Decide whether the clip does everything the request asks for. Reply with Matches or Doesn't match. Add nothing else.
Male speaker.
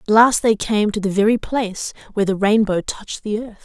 Doesn't match